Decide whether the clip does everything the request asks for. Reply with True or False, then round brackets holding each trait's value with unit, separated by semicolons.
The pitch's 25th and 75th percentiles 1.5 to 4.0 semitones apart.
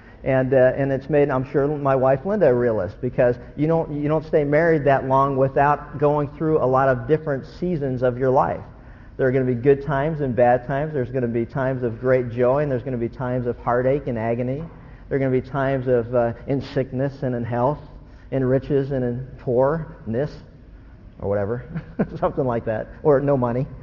True (2.6 semitones)